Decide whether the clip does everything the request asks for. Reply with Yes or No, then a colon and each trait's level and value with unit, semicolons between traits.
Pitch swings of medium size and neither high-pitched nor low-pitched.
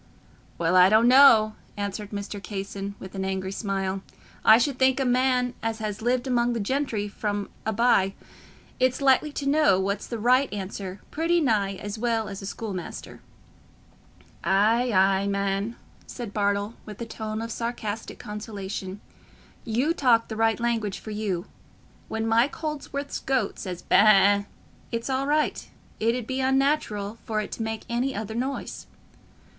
No: average, 3.7 semitones; high, 220 Hz